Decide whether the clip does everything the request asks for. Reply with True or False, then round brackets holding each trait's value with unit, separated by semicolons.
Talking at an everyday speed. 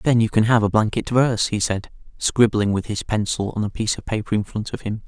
False (260 wpm)